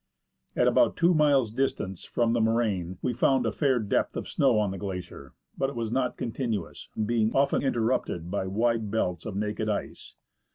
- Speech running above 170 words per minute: Yes, average, 180 wpm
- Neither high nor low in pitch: No, low, 110 Hz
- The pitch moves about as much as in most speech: Yes, average, 3.8 semitones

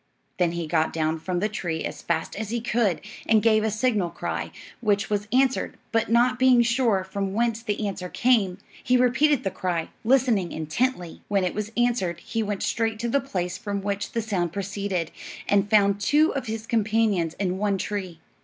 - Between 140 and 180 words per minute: No, average, 190 wpm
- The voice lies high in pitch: Yes, high, 205 Hz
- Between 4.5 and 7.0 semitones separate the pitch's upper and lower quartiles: No, average, 4.0 semitones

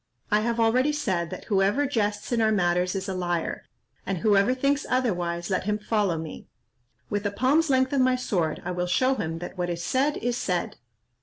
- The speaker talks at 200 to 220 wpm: Yes, fast, 205 wpm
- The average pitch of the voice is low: No, high, 205 Hz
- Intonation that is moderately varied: No, wide, 6.2 semitones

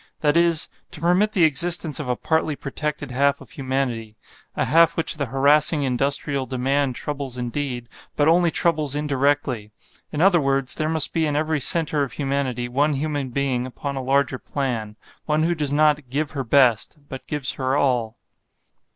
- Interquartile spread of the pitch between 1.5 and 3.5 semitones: Yes, average, 2.8 semitones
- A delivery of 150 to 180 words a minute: Yes, average, 175 wpm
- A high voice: No, medium, 140 Hz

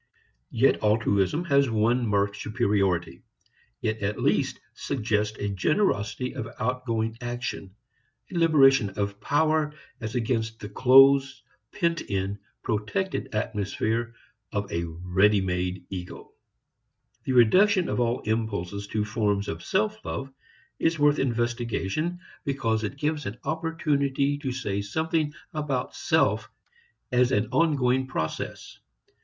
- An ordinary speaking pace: No, slow, 120 wpm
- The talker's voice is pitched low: Yes, low, 120 Hz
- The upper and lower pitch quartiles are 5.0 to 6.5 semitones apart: Yes, wide, 5.4 semitones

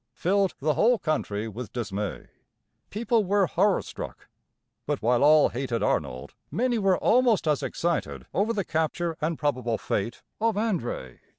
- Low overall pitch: No, medium, 160 Hz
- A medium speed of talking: Yes, average, 150 wpm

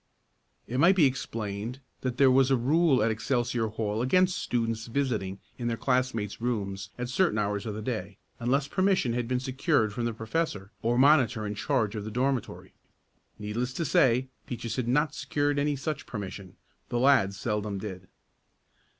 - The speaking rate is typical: Yes, average, 170 wpm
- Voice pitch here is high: No, low, 120 Hz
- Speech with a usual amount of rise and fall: Yes, average, 4.0 semitones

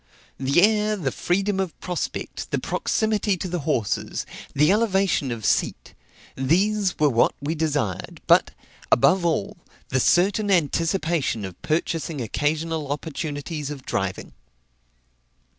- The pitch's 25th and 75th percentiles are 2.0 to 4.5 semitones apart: No, wide, 5.4 semitones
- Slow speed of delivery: Yes, slow, 125 wpm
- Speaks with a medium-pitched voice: Yes, medium, 160 Hz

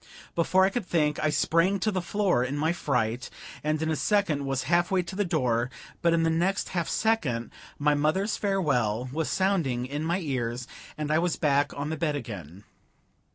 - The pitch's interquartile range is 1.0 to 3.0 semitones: No, average, 5.2 semitones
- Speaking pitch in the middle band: Yes, medium, 155 Hz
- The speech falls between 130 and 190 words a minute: No, average, 200 wpm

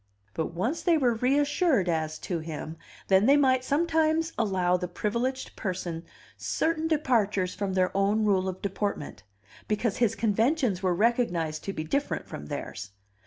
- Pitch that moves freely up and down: Yes, wide, 6.6 semitones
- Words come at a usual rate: Yes, average, 155 wpm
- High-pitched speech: Yes, high, 205 Hz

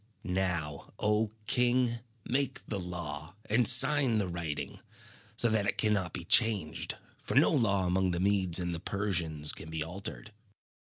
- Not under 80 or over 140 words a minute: No, average, 155 wpm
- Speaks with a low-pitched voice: Yes, very low, 95 Hz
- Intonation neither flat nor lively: Yes, average, 4.2 semitones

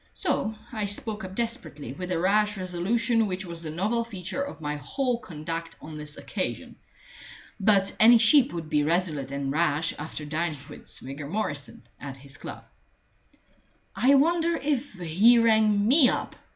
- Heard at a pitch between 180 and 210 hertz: Yes, medium, 185 Hz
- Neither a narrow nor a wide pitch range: No, wide, 6.9 semitones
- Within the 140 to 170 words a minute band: Yes, average, 160 wpm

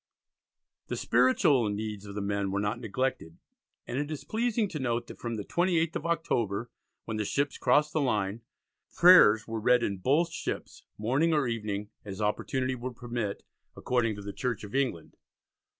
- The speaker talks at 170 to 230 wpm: Yes, average, 175 wpm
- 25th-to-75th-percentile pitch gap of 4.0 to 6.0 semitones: Yes, average, 5.2 semitones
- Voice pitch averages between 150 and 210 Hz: No, low, 120 Hz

